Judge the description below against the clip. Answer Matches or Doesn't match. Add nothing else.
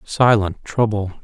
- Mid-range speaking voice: Doesn't match